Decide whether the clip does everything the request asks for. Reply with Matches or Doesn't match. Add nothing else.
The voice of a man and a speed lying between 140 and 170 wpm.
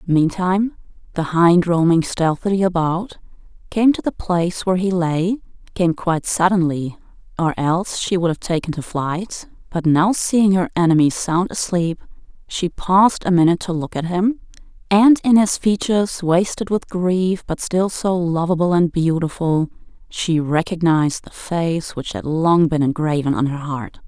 Doesn't match